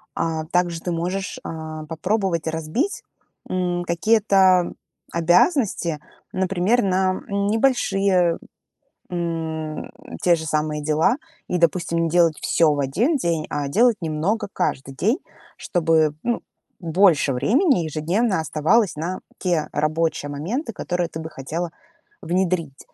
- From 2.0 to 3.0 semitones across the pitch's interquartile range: No, average, 3.4 semitones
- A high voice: No, medium, 170 Hz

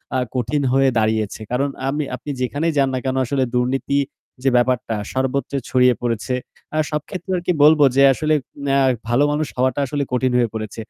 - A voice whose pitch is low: Yes, low, 130 Hz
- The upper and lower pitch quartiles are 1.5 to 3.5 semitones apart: Yes, narrow, 2.6 semitones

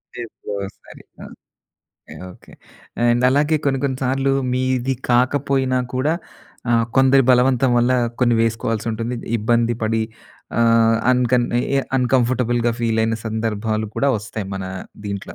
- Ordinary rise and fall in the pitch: No, narrow, 2.3 semitones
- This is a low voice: Yes, low, 120 Hz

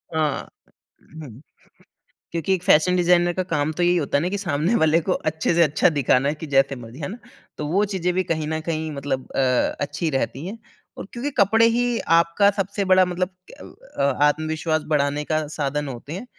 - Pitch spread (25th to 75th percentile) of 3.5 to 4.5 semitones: Yes, average, 4.1 semitones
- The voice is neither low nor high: Yes, medium, 160 Hz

